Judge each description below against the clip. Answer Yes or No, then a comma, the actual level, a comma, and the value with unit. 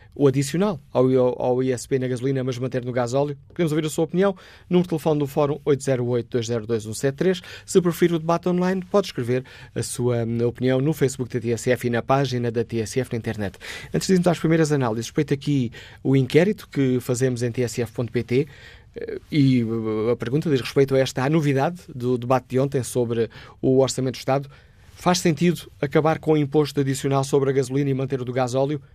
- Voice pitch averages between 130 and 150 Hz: Yes, low, 135 Hz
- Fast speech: Yes, fast, 190 wpm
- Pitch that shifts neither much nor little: Yes, average, 3.7 semitones